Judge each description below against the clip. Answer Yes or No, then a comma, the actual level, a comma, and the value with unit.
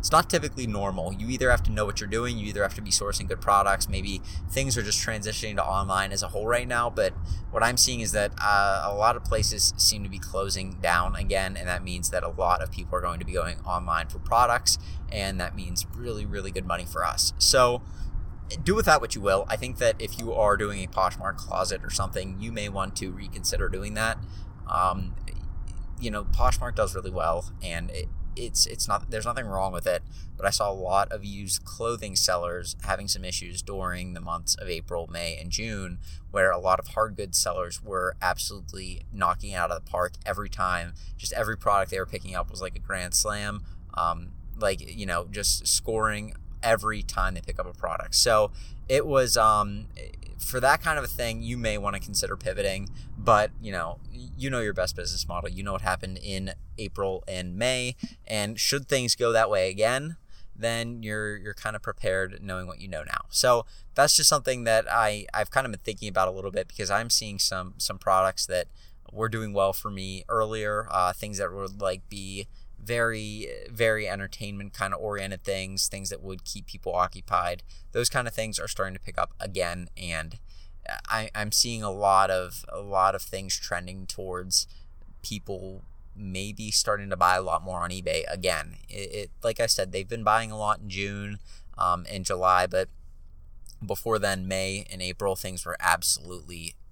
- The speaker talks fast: Yes, fast, 210 wpm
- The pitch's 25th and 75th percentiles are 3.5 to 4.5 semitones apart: No, average, 3.0 semitones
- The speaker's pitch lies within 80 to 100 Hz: Yes, very low, 95 Hz